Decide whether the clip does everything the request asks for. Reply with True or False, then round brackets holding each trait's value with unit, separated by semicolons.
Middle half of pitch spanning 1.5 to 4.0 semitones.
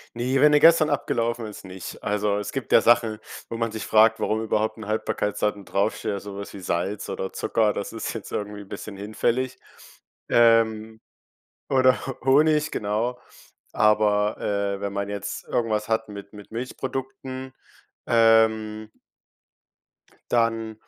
True (2.4 semitones)